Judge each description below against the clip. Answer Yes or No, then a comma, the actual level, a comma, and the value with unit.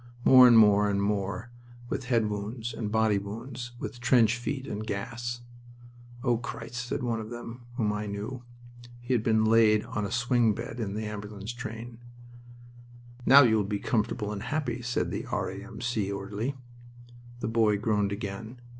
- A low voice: Yes, low, 110 Hz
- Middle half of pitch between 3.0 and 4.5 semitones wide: No, narrow, 2.5 semitones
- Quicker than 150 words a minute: Yes, average, 165 wpm